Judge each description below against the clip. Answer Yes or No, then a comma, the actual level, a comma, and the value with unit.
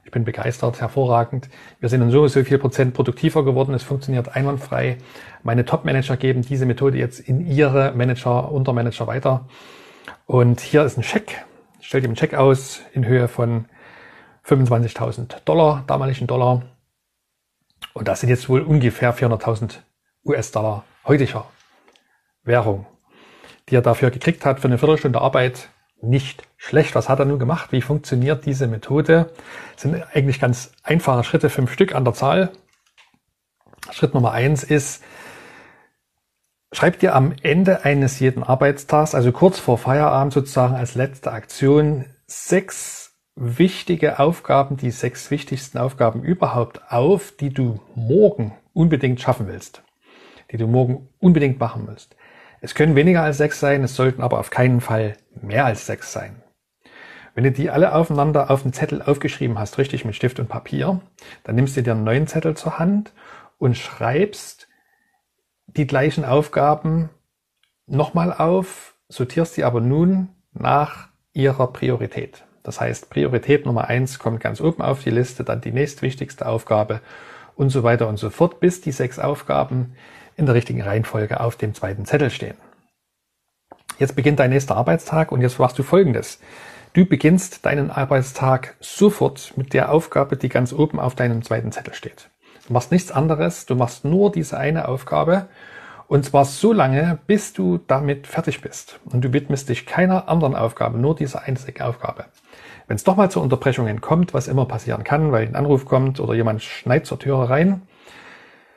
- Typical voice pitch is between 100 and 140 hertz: Yes, low, 135 Hz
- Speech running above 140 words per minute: Yes, average, 160 wpm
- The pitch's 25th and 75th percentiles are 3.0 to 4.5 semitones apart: Yes, average, 3.7 semitones